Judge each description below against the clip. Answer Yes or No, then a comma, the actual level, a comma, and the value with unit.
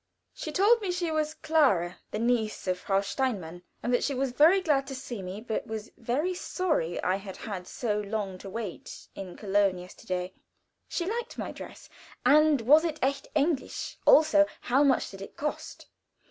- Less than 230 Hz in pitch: No, high, 245 Hz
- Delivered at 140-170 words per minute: No, average, 180 wpm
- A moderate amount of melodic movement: No, wide, 7.6 semitones